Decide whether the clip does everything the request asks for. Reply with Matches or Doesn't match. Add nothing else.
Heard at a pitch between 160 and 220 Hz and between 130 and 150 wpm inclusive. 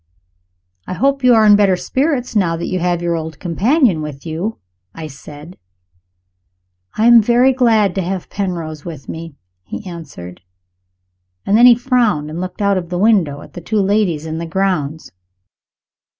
Doesn't match